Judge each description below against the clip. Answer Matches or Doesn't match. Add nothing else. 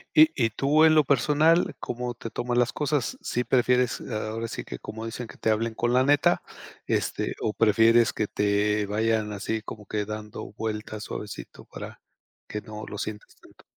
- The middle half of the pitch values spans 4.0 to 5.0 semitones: Doesn't match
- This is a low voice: Matches